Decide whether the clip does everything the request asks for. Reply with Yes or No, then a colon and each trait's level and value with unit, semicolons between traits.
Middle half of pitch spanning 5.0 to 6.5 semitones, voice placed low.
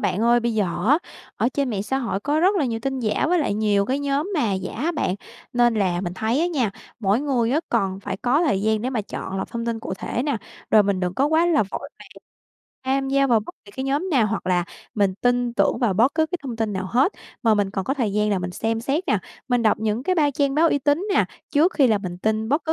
No: average, 5.3 semitones; high, 235 Hz